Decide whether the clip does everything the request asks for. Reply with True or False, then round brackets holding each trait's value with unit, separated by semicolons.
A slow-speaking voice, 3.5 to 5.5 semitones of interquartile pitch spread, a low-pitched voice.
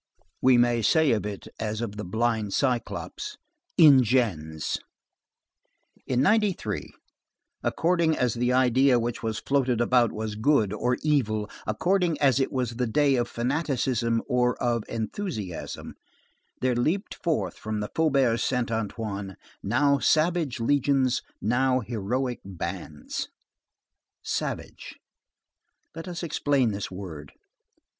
True (120 wpm; 4.3 semitones; 125 Hz)